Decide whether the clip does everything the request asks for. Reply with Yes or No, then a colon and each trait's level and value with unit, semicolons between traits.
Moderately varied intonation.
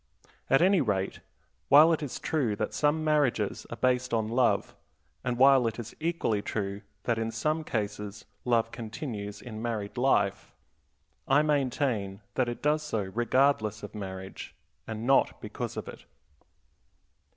Yes: average, 4.7 semitones